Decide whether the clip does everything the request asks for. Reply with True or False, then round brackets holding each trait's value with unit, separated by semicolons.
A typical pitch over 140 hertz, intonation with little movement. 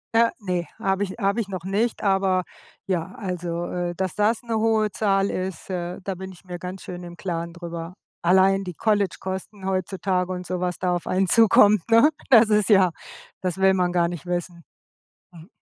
True (185 Hz; 2.0 semitones)